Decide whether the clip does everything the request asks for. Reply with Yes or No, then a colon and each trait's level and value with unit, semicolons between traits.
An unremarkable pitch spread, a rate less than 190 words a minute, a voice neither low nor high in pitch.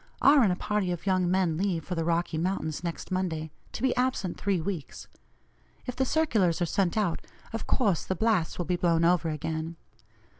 No: average, 3.5 semitones; average, 195 wpm; medium, 180 Hz